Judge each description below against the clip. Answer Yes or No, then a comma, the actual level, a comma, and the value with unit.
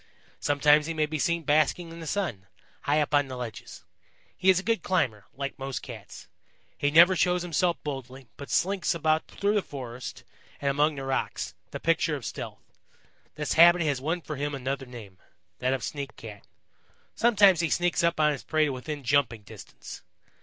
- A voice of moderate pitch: Yes, medium, 150 Hz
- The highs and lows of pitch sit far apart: No, average, 4.0 semitones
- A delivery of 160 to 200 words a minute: Yes, average, 190 wpm